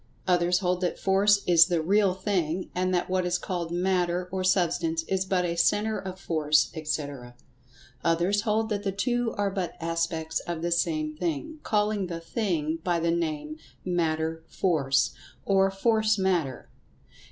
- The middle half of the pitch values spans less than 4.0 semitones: Yes, average, 2.8 semitones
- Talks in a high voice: No, medium, 180 Hz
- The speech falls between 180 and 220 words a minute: No, average, 160 wpm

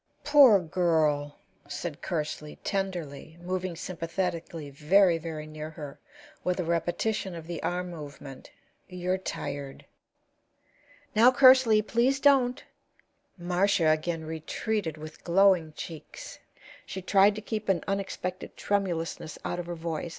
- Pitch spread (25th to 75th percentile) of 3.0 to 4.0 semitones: Yes, average, 3.7 semitones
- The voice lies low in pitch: No, medium, 175 Hz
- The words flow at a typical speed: No, slow, 120 wpm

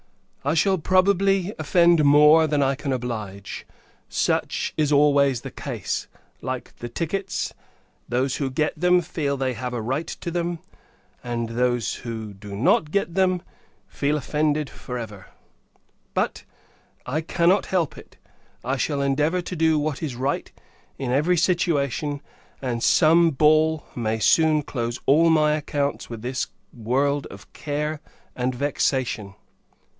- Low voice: No, medium, 145 Hz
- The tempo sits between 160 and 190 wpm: No, average, 145 wpm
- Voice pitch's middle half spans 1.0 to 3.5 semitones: No, average, 4.2 semitones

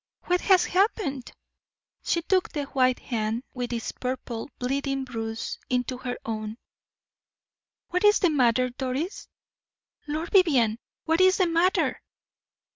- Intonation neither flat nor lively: No, wide, 6.0 semitones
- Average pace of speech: No, slow, 125 wpm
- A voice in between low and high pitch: No, very high, 265 Hz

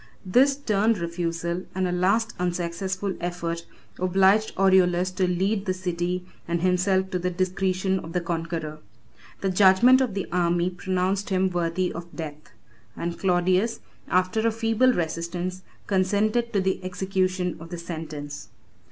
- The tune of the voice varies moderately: No, narrow, 1.9 semitones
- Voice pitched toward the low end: No, medium, 185 Hz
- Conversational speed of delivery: Yes, average, 145 wpm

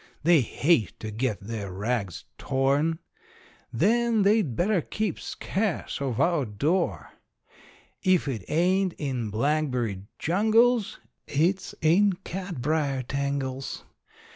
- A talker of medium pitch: Yes, medium, 150 Hz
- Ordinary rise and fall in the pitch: No, wide, 6.8 semitones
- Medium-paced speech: No, slow, 105 wpm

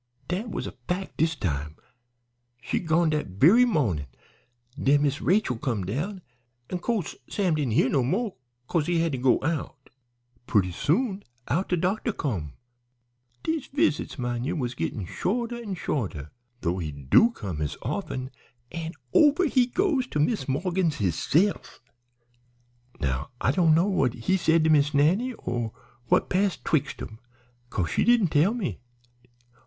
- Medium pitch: Yes, medium, 155 Hz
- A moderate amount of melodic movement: No, wide, 8.0 semitones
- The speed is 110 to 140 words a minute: No, average, 160 wpm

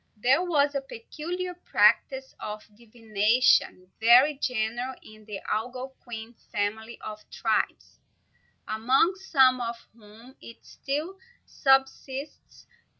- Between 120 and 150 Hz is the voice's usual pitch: No, very high, 250 Hz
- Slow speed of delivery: Yes, slow, 100 wpm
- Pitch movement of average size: Yes, average, 3.8 semitones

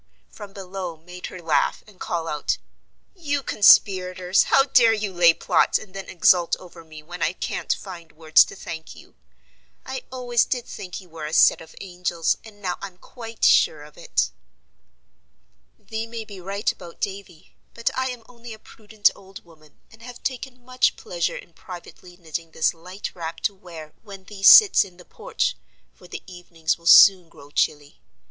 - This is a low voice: No, medium, 185 Hz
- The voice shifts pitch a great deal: No, average, 4.5 semitones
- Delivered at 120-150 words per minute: No, average, 180 wpm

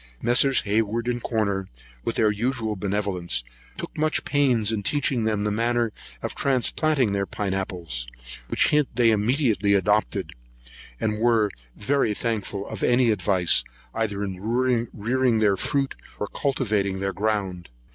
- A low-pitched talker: Yes, low, 110 Hz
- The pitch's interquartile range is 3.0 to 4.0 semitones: Yes, average, 3.4 semitones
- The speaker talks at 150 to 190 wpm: No, average, 140 wpm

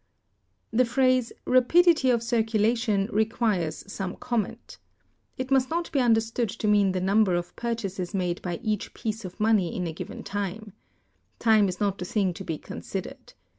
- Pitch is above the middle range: Yes, high, 215 Hz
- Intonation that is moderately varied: Yes, average, 3.8 semitones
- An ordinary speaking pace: Yes, average, 165 wpm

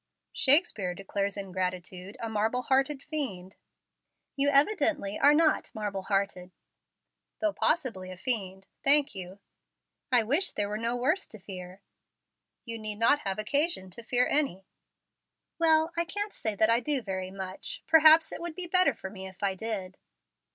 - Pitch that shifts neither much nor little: No, wide, 7.3 semitones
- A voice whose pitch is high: Yes, high, 220 Hz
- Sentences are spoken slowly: No, average, 160 wpm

